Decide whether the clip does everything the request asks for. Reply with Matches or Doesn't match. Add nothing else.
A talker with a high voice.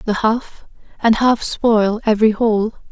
Matches